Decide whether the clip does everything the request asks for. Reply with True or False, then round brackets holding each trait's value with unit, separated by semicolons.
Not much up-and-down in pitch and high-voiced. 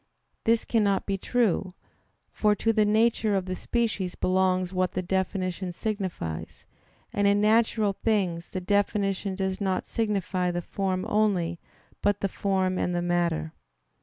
True (2.3 semitones; 195 Hz)